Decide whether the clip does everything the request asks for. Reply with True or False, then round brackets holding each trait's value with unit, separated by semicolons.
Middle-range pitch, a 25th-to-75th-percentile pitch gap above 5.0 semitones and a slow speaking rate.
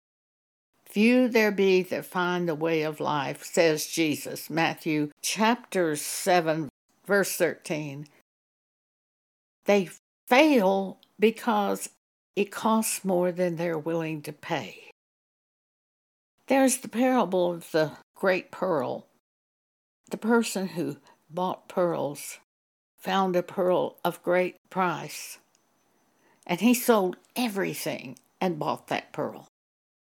True (180 Hz; 5.4 semitones; 105 wpm)